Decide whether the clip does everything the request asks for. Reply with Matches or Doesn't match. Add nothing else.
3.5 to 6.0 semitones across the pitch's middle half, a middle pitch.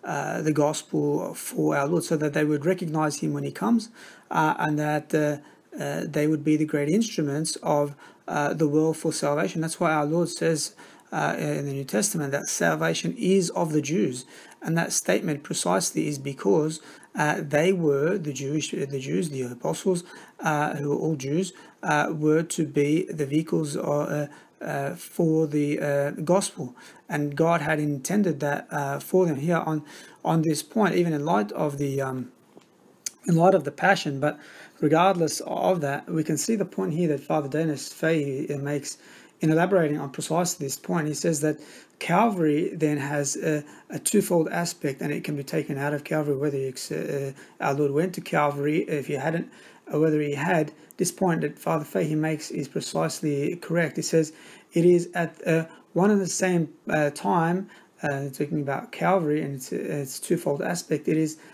Doesn't match